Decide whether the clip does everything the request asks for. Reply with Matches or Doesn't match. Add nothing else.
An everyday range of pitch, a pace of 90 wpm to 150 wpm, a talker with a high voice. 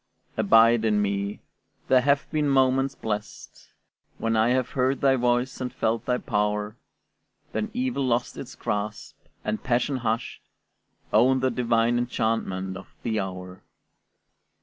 Doesn't match